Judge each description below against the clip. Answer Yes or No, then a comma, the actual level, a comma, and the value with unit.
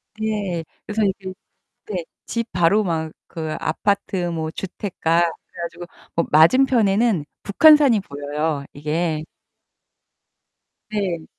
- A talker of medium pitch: Yes, medium, 175 Hz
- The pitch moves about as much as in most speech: Yes, average, 4.5 semitones